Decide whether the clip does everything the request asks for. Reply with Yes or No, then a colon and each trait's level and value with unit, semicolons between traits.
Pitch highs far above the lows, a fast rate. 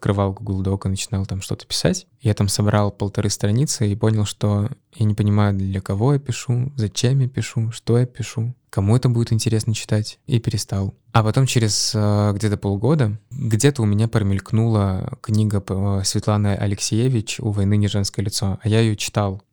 No: narrow, 2.5 semitones; fast, 175 wpm